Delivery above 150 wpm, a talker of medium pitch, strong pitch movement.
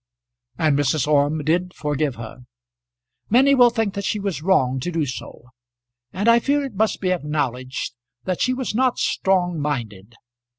Yes: average, 165 wpm; medium, 165 Hz; wide, 6.5 semitones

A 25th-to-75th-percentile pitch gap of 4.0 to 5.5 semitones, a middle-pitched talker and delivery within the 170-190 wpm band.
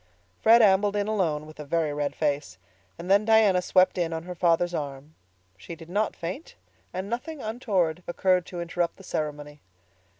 Yes: average, 4.4 semitones; medium, 175 Hz; average, 175 wpm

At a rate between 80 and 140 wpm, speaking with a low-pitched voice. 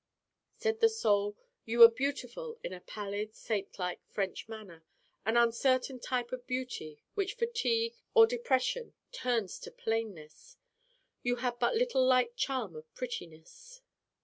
No: slow, 135 wpm; high, 245 Hz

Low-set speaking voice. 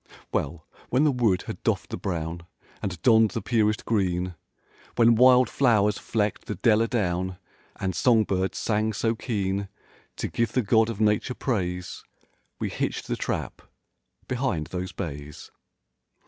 Yes: low, 105 Hz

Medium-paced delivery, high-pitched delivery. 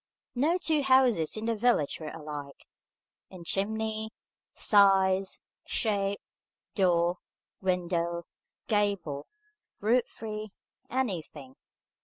No: slow, 90 wpm; high, 195 Hz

